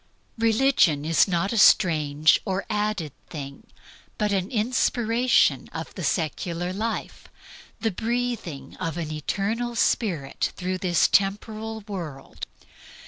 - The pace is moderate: No, slow, 115 wpm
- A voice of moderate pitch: No, high, 195 Hz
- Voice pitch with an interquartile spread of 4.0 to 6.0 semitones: Yes, wide, 5.4 semitones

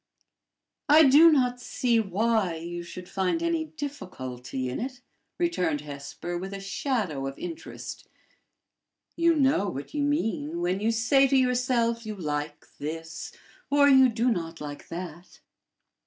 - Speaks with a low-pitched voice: No, high, 215 Hz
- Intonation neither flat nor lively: No, wide, 8.3 semitones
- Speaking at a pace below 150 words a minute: Yes, average, 140 wpm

